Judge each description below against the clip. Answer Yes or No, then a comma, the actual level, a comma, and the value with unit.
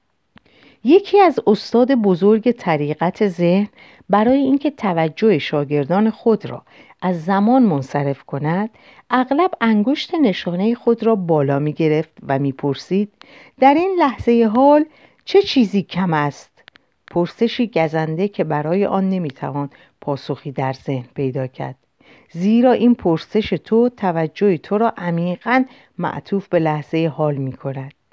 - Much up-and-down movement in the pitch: Yes, wide, 7.4 semitones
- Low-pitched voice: No, high, 195 Hz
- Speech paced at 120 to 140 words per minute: Yes, average, 130 wpm